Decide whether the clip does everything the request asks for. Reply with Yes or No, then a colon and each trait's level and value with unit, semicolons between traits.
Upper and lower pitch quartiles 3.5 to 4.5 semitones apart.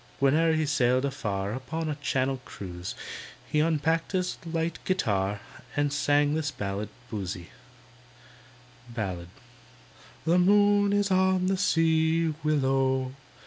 No: average, 5.1 semitones